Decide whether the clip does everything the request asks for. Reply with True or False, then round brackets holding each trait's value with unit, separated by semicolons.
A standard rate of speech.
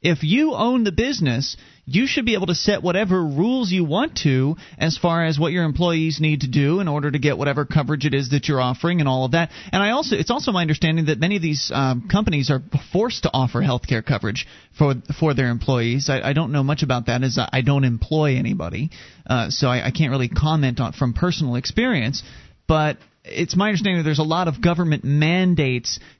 False (225 wpm)